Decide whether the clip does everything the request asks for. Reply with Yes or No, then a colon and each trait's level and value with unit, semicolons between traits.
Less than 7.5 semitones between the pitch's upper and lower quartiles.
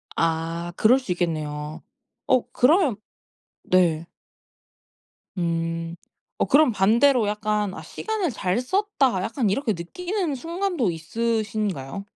No: wide, 7.9 semitones